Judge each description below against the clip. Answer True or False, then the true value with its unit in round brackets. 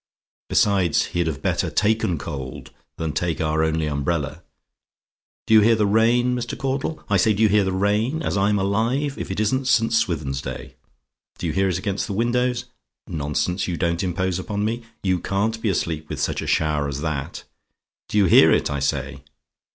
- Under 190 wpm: False (195 wpm)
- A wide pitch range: True (5.8 semitones)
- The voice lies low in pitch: True (95 Hz)